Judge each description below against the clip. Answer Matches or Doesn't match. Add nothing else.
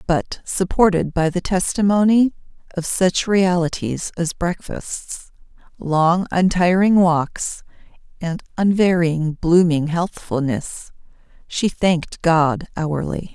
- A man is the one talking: Doesn't match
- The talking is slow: Matches